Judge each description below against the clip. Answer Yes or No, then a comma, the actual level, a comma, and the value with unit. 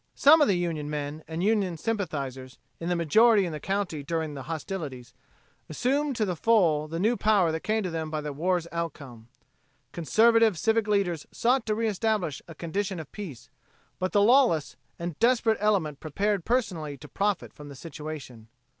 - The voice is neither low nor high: Yes, medium, 175 Hz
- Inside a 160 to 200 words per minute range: Yes, average, 170 wpm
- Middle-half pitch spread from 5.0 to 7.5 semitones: Yes, wide, 5.6 semitones